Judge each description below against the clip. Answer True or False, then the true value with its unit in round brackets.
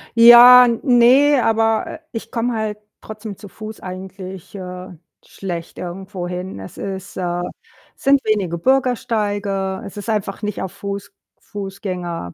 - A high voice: True (200 Hz)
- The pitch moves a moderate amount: True (3.4 semitones)